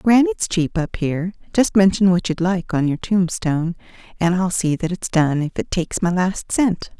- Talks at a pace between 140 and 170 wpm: No, fast, 205 wpm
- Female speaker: Yes, female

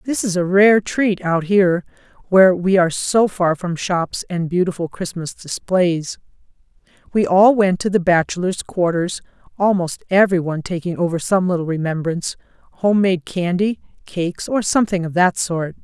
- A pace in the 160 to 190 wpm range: No, average, 150 wpm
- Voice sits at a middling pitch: Yes, medium, 180 Hz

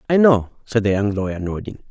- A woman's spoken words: No, male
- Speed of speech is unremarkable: No, fast, 220 wpm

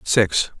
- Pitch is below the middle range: Yes, low, 100 Hz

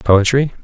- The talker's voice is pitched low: Yes, low, 120 Hz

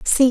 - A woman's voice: Yes, female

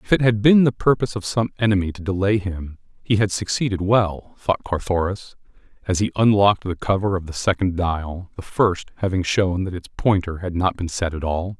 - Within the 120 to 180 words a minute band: No, fast, 205 wpm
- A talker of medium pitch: No, very low, 95 Hz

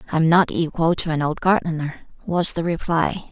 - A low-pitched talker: No, medium, 165 Hz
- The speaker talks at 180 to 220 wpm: Yes, average, 200 wpm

